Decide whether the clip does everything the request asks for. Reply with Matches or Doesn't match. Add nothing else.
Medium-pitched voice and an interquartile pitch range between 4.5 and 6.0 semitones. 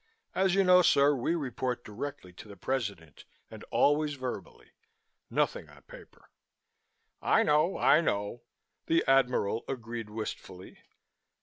Doesn't match